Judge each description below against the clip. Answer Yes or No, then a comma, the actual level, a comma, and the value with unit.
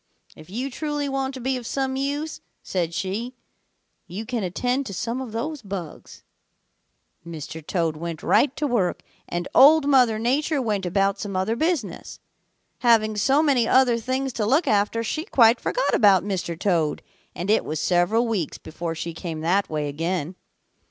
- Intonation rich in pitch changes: Yes, wide, 6.9 semitones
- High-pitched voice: Yes, high, 220 Hz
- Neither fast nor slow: Yes, average, 170 wpm